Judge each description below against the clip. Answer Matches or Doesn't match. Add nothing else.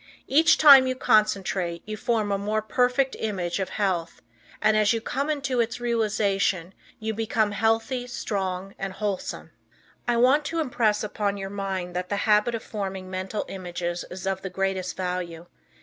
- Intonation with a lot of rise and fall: Doesn't match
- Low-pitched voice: Doesn't match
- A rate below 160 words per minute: Doesn't match